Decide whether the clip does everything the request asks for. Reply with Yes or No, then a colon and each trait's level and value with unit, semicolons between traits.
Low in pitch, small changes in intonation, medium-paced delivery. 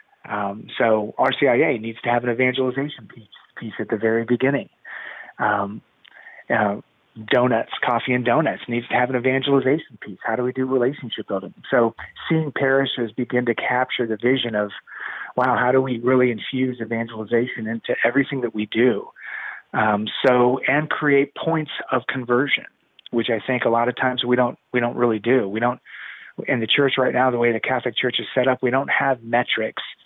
Yes: low, 125 Hz; narrow, 2.0 semitones; average, 185 wpm